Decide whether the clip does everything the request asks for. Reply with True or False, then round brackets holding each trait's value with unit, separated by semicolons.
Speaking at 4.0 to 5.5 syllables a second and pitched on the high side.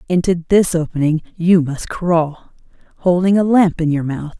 False (4.5 syllables/s; 170 Hz)